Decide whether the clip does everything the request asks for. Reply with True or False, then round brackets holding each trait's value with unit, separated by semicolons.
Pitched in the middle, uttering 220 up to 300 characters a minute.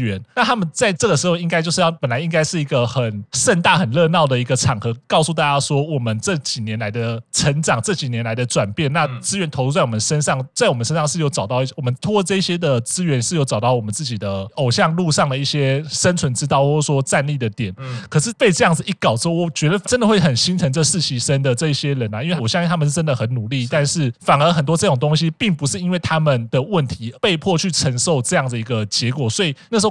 False (145 Hz; 370 characters per minute)